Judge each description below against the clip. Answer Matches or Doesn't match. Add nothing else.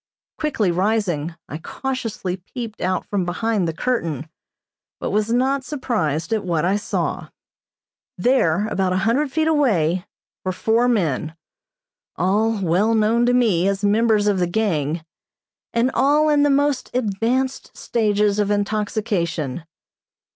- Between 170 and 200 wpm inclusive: Doesn't match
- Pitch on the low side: Doesn't match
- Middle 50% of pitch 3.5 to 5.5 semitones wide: Matches